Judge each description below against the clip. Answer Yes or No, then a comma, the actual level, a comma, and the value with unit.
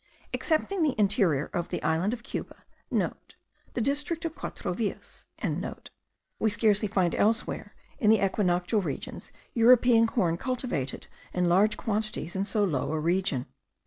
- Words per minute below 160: Yes, average, 145 wpm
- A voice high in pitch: Yes, high, 210 Hz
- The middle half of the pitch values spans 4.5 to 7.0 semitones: Yes, average, 4.9 semitones